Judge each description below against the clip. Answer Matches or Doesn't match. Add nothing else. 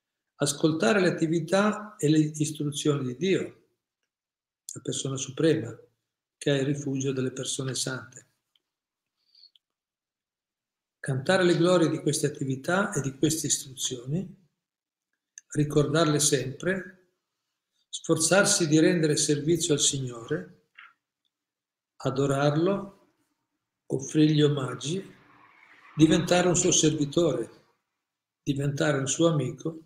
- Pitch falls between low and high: Matches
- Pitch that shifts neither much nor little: Matches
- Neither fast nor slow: Doesn't match